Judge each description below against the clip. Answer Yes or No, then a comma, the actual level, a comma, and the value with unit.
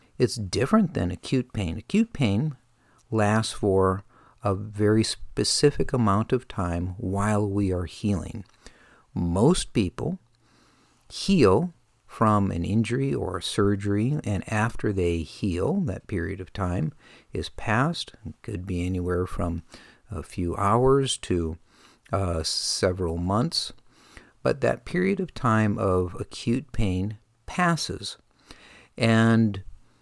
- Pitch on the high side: No, low, 105 Hz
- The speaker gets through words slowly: Yes, slow, 120 wpm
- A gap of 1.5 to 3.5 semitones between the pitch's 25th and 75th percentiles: No, average, 4.6 semitones